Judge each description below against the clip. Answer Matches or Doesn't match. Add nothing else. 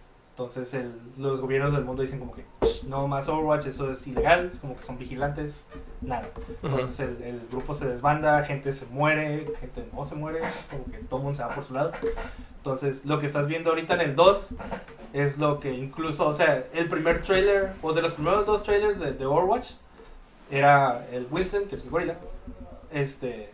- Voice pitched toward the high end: Doesn't match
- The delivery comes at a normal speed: Doesn't match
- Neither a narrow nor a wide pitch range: Matches